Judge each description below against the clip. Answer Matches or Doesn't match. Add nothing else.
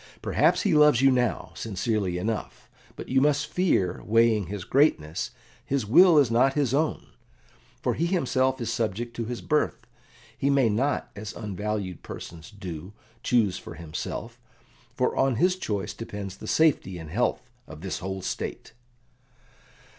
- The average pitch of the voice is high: Doesn't match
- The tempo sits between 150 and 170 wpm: Matches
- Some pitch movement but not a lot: Doesn't match